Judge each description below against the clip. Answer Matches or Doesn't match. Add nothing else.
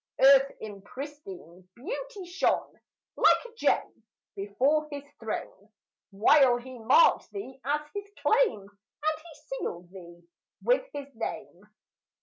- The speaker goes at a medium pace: Doesn't match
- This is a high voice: Matches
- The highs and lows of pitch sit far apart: Matches